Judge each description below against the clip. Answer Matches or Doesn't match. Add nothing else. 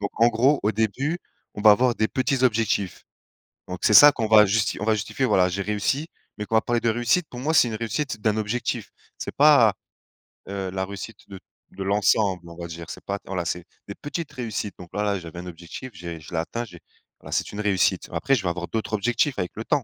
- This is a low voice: Matches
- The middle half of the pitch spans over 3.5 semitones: Matches